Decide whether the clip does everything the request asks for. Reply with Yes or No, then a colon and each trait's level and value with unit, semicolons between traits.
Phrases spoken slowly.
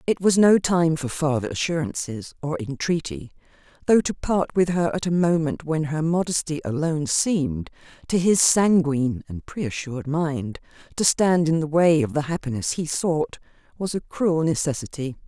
No: average, 165 wpm